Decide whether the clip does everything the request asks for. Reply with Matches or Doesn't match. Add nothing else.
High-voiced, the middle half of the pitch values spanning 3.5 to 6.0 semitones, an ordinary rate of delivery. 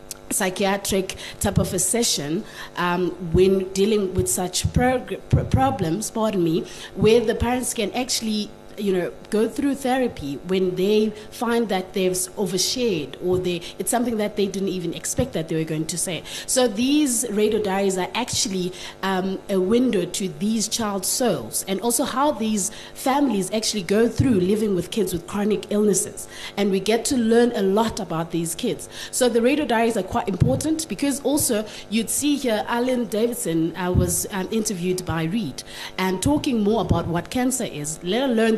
Matches